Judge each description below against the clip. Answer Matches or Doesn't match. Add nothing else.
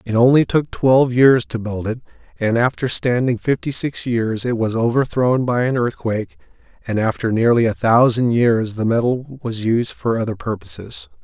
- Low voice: Matches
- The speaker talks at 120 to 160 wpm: Doesn't match